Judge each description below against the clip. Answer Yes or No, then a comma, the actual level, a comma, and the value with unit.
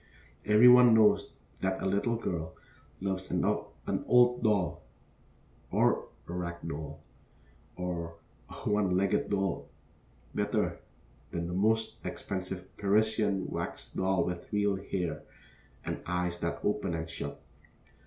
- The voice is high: No, very low, 95 Hz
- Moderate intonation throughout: Yes, average, 3.0 semitones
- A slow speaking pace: Yes, slow, 125 wpm